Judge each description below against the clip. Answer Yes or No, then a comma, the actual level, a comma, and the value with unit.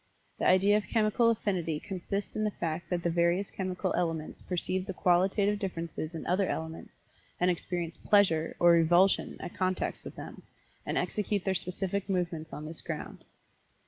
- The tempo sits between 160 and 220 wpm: Yes, average, 165 wpm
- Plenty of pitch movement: No, average, 2.7 semitones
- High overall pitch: No, medium, 180 Hz